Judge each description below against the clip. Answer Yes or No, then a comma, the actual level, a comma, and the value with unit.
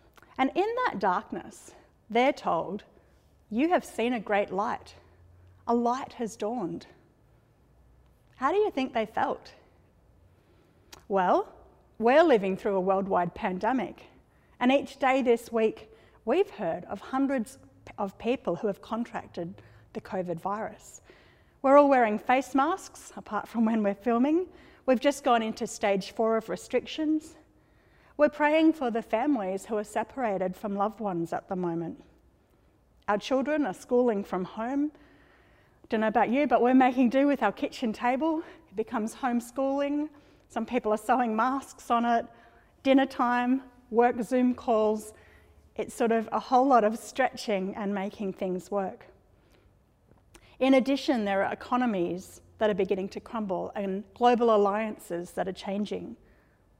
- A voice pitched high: Yes, high, 235 Hz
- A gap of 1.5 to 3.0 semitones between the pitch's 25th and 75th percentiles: No, average, 4.5 semitones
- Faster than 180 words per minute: No, average, 145 wpm